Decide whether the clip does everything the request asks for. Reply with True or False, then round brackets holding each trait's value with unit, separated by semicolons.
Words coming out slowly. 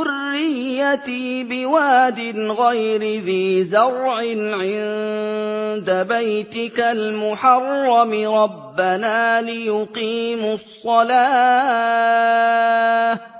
True (50 wpm)